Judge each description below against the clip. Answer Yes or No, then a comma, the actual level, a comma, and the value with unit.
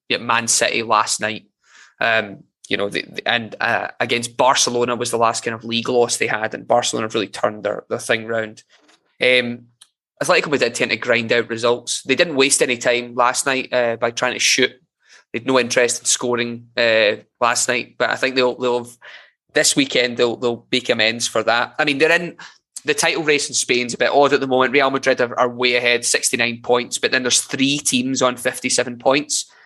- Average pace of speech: No, fast, 225 wpm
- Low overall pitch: Yes, low, 125 Hz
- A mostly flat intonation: Yes, narrow, 1.9 semitones